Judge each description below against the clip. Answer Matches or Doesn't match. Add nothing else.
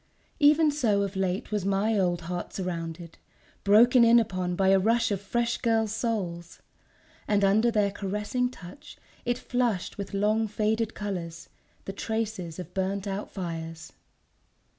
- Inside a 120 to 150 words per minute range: Matches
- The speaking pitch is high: Matches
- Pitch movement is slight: Doesn't match